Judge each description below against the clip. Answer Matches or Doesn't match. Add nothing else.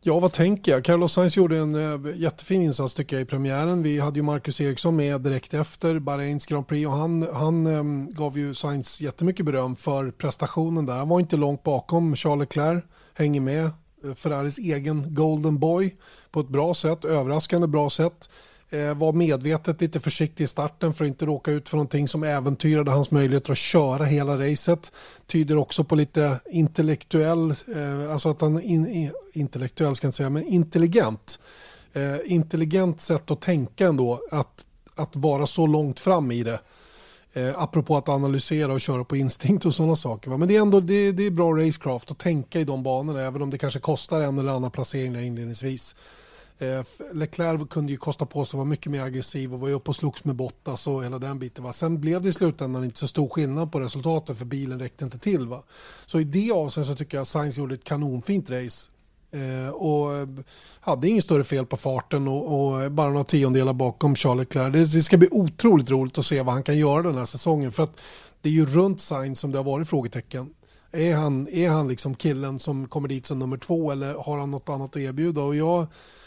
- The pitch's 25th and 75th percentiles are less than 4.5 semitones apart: Matches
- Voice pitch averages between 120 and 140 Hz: Doesn't match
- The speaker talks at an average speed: Doesn't match